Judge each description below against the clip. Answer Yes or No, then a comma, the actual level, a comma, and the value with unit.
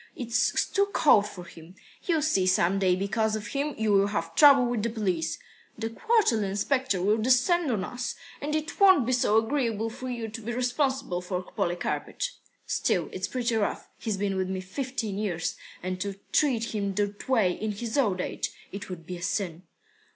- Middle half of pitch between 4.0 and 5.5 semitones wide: Yes, average, 4.9 semitones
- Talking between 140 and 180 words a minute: No, average, 190 wpm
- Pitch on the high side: Yes, high, 220 Hz